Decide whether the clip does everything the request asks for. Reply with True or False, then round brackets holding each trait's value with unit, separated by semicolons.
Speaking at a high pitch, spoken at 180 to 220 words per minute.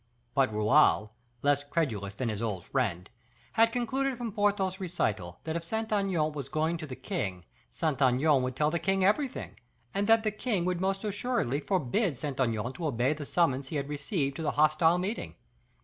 False (155 Hz; 190 wpm)